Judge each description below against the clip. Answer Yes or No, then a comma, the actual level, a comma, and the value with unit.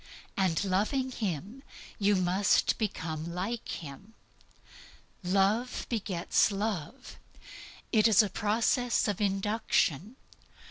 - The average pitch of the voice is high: Yes, high, 205 Hz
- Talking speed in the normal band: No, slow, 95 wpm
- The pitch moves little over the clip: No, average, 3.4 semitones